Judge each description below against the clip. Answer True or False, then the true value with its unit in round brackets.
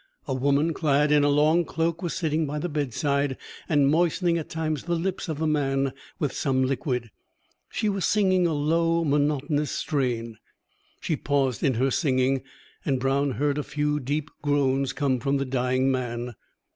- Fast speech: False (170 wpm)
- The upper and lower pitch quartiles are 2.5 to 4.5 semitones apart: True (2.8 semitones)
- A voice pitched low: False (145 Hz)